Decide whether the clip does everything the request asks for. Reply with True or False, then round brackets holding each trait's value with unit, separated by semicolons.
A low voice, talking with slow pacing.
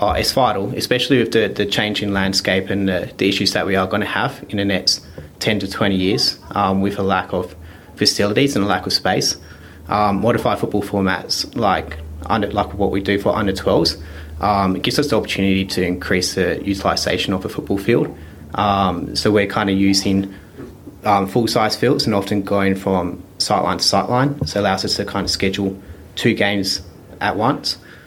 False (100 Hz; 200 wpm)